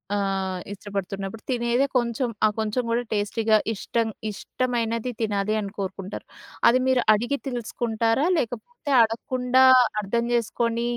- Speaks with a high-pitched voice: Yes, high, 230 Hz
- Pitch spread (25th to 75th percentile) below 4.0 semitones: Yes, average, 2.8 semitones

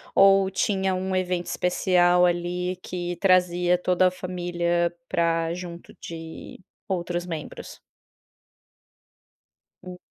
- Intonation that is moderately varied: No, narrow, 1.0 semitones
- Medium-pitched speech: Yes, medium, 180 Hz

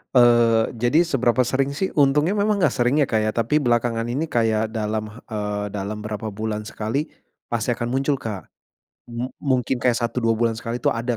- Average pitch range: Yes, average, 3.0 semitones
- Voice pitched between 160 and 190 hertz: No, low, 120 Hz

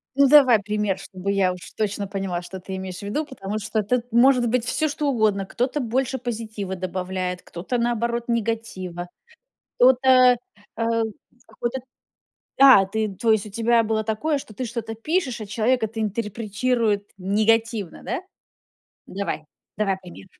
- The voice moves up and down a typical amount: Yes, average, 3.5 semitones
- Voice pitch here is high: Yes, high, 220 Hz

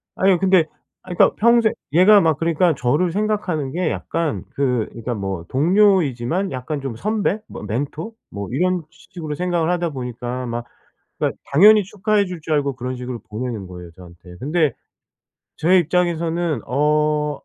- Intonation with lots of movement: Yes, wide, 6.3 semitones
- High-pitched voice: No, medium, 155 Hz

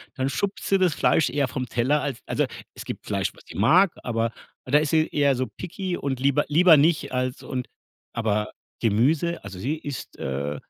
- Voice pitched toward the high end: No, medium, 140 Hz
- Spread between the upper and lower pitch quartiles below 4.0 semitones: No, average, 5.0 semitones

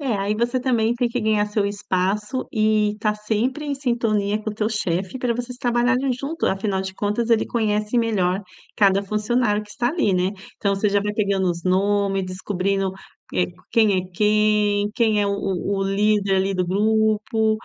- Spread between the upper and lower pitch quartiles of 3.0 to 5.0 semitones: No, narrow, 2.5 semitones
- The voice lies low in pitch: No, high, 210 Hz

